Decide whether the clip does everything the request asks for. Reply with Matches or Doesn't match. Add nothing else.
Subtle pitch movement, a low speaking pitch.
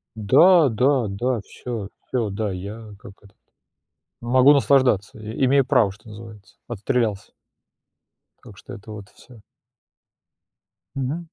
Doesn't match